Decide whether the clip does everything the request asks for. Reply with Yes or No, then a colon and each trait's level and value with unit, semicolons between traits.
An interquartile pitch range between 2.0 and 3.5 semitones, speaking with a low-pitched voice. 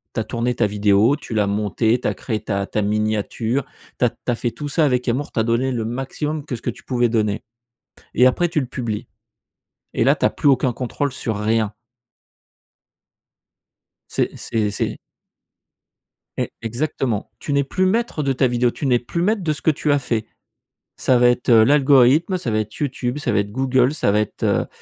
No: average, 4.2 semitones; low, 125 Hz